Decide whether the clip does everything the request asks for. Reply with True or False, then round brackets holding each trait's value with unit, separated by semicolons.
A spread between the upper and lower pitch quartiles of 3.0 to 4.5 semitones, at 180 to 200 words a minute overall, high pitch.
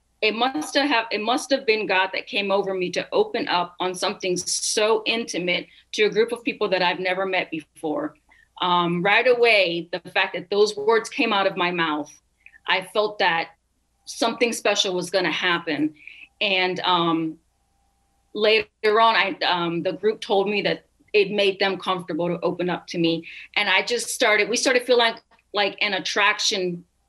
True (3.8 semitones; 185 wpm; 195 Hz)